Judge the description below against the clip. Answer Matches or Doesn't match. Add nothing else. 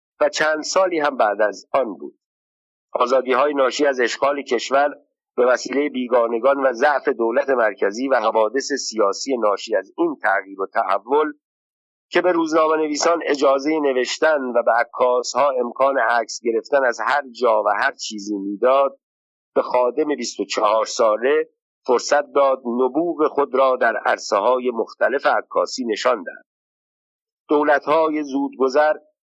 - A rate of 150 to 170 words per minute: Doesn't match